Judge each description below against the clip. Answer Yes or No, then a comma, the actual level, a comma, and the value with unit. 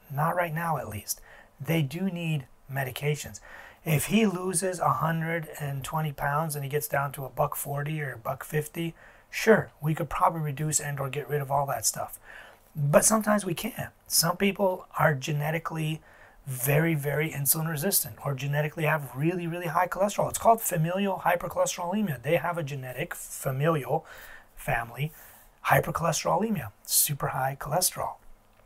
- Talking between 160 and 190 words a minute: No, average, 150 wpm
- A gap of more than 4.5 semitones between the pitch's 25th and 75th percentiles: No, average, 3.7 semitones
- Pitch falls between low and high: Yes, medium, 155 Hz